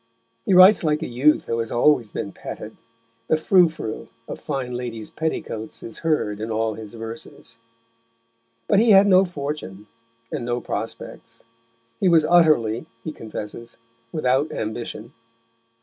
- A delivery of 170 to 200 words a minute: No, average, 145 wpm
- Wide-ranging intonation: Yes, wide, 6.0 semitones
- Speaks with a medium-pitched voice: No, low, 125 Hz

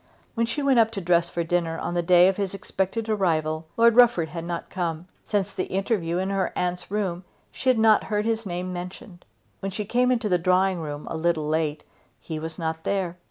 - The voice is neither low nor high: Yes, medium, 180 Hz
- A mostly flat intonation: No, average, 3.7 semitones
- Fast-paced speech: Yes, fast, 215 wpm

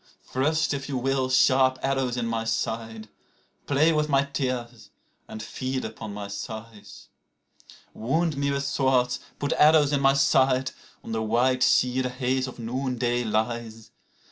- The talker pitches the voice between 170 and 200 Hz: No, low, 130 Hz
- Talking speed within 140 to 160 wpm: Yes, average, 155 wpm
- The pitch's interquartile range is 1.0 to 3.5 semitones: Yes, average, 2.9 semitones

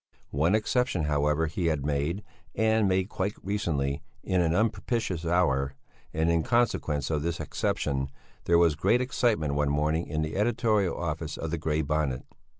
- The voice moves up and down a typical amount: Yes, average, 4.9 semitones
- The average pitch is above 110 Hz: No, very low, 80 Hz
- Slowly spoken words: No, average, 160 wpm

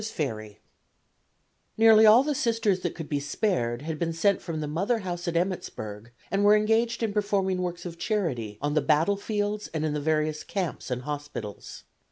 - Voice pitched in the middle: Yes, medium, 175 Hz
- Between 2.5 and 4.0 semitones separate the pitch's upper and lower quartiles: No, wide, 5.6 semitones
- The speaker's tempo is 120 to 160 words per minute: No, average, 180 wpm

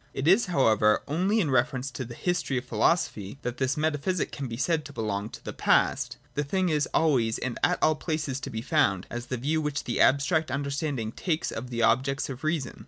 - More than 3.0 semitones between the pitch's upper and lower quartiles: Yes, average, 4.5 semitones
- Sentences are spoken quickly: Yes, fast, 220 wpm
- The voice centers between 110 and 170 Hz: Yes, medium, 140 Hz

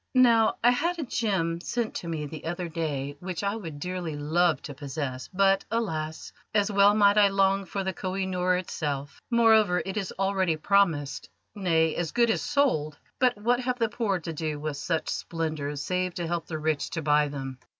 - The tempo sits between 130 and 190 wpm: No, average, 200 wpm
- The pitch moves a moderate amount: Yes, average, 4.8 semitones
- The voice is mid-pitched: Yes, medium, 180 Hz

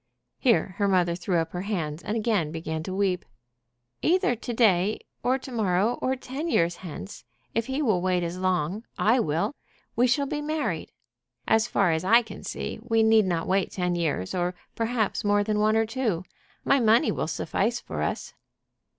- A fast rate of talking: No, average, 185 wpm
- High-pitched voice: Yes, high, 205 Hz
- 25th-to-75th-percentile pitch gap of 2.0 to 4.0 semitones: No, average, 4.9 semitones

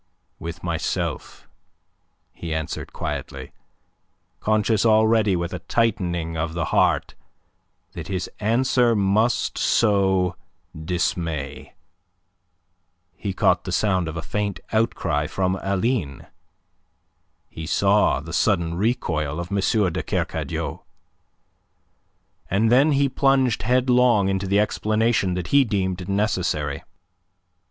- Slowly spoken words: Yes, slow, 110 wpm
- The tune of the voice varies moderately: Yes, average, 4.4 semitones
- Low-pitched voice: Yes, very low, 95 Hz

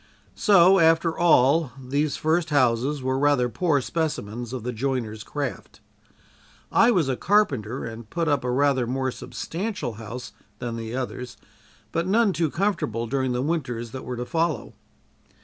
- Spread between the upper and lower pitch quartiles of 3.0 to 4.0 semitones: No, average, 5.1 semitones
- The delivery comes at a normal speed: Yes, average, 155 wpm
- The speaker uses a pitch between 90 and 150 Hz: Yes, low, 135 Hz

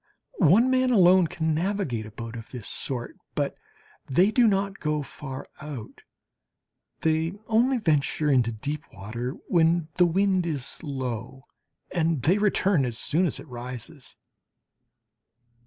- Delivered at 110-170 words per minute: Yes, average, 140 wpm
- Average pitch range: No, wide, 6.6 semitones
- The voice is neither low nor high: Yes, medium, 155 Hz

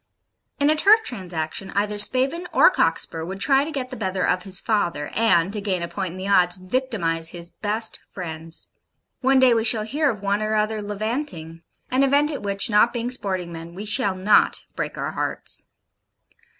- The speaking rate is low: No, average, 190 wpm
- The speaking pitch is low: No, high, 205 Hz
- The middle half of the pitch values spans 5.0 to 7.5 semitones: Yes, wide, 5.6 semitones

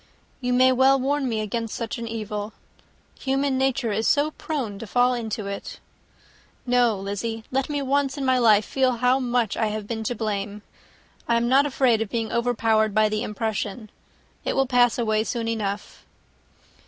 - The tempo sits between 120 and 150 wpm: No, average, 180 wpm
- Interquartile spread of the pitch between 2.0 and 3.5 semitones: Yes, average, 3.1 semitones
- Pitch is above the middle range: Yes, high, 235 Hz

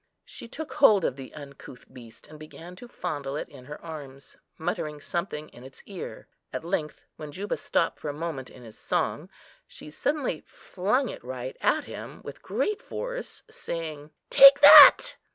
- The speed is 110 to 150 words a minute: No, average, 170 wpm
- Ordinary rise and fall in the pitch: No, wide, 6.0 semitones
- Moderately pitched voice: Yes, medium, 155 Hz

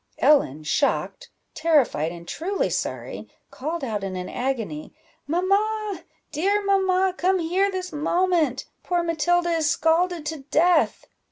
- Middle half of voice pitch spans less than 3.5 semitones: No, average, 5.2 semitones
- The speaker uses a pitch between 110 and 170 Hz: No, very high, 330 Hz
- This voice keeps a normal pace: No, slow, 125 wpm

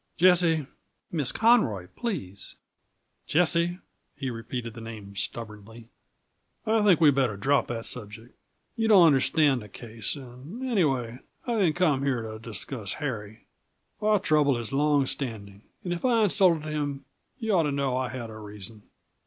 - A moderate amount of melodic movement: No, wide, 6.9 semitones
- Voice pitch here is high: No, low, 135 Hz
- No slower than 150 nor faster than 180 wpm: Yes, average, 155 wpm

